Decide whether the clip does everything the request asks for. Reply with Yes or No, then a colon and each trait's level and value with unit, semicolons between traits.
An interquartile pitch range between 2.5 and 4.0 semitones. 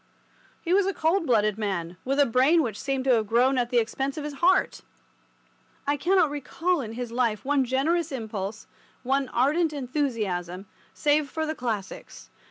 No: average, 5.0 semitones